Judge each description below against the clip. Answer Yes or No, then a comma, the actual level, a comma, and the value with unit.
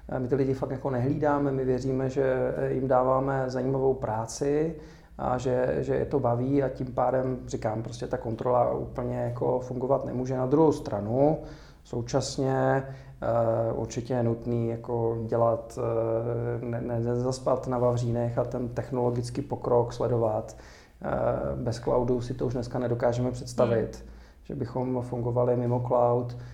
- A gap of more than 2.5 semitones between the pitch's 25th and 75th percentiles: No, narrow, 1.8 semitones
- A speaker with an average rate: Yes, average, 140 wpm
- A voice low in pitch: Yes, low, 125 Hz